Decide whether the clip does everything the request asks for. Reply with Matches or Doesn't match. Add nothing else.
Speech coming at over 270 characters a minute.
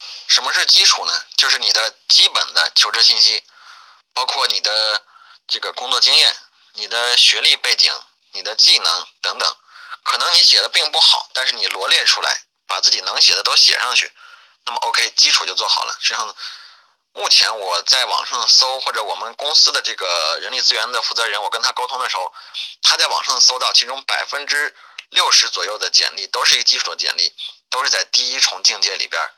Matches